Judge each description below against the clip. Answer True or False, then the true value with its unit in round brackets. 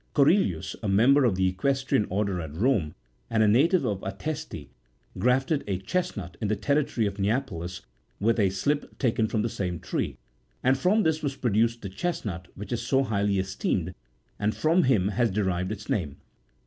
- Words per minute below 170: False (175 wpm)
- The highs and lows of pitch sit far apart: True (5.9 semitones)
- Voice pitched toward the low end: True (110 Hz)